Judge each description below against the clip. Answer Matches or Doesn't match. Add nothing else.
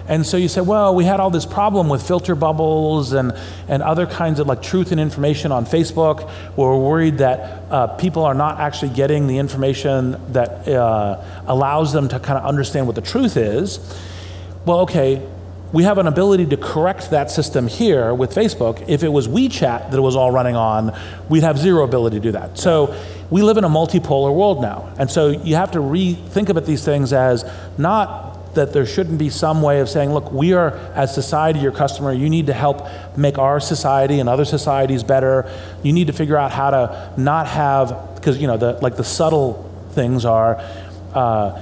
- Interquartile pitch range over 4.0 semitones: Matches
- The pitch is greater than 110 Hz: Matches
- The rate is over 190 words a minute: Matches